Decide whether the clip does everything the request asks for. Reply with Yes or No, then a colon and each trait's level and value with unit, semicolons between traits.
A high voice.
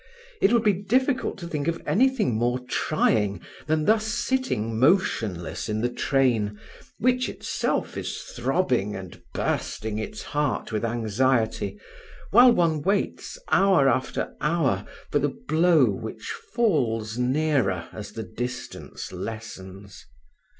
No: low, 130 Hz